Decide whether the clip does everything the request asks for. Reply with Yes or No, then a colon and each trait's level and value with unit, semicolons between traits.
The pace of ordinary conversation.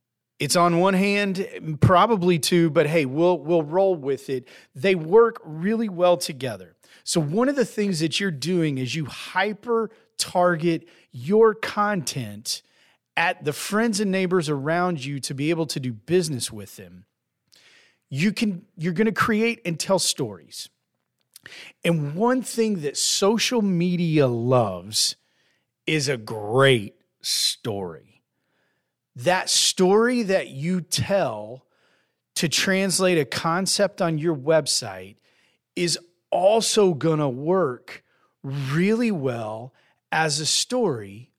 No: slow, 130 wpm